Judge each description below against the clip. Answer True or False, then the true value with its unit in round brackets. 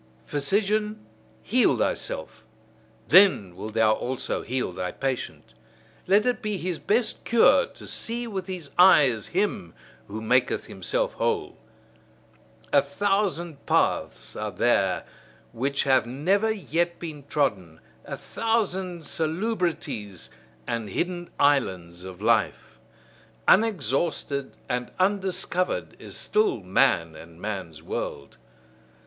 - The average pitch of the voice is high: False (160 Hz)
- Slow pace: True (110 wpm)